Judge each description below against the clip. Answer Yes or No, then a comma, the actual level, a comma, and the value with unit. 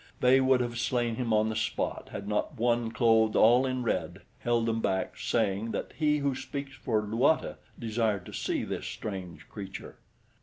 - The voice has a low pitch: Yes, low, 115 Hz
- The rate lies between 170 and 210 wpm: Yes, average, 180 wpm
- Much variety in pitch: No, average, 2.8 semitones